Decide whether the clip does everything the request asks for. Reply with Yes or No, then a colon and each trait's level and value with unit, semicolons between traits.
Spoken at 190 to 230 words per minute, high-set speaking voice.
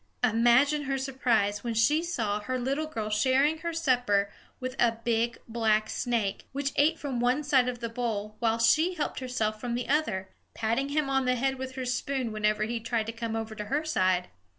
Yes: average, 200 wpm; high, 240 Hz